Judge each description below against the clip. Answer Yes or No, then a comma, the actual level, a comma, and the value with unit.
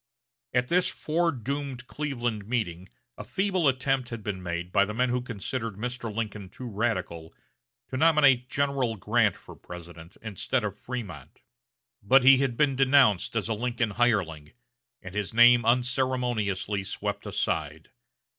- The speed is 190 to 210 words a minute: No, average, 145 wpm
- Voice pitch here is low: Yes, low, 120 Hz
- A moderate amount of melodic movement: Yes, average, 4.5 semitones